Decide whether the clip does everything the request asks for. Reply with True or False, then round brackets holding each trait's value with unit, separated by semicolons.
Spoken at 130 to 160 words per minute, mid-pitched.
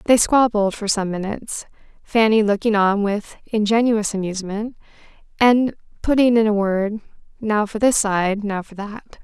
False (150 wpm; 210 Hz)